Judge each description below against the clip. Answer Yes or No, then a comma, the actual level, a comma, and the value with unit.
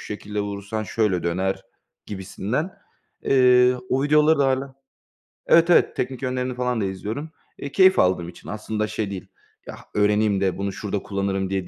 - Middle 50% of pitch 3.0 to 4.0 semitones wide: No, average, 4.8 semitones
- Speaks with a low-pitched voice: Yes, low, 105 Hz